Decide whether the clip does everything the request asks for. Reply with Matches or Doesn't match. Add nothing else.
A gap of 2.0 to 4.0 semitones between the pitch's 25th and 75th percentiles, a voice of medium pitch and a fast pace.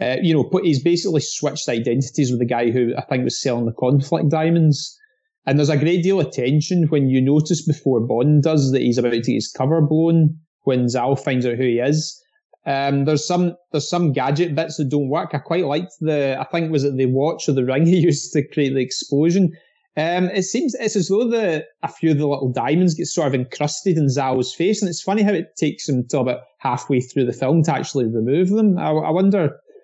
Doesn't match